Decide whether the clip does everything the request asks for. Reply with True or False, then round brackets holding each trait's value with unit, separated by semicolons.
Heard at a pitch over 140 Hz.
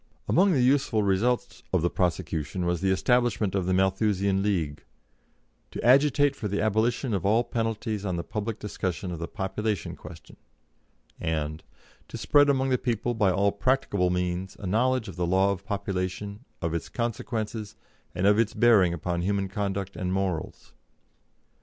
False (100 Hz)